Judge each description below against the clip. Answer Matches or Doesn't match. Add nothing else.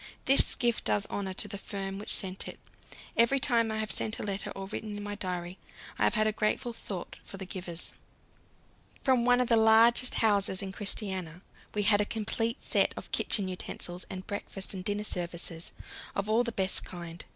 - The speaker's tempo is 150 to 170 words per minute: Doesn't match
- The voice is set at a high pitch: Matches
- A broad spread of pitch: Doesn't match